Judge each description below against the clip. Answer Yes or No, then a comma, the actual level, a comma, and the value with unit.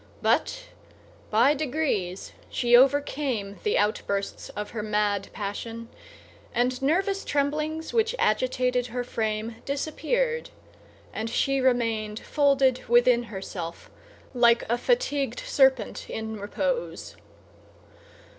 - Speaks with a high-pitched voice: Yes, very high, 250 Hz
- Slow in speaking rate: Yes, slow, 100 wpm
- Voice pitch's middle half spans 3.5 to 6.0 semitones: Yes, average, 5.0 semitones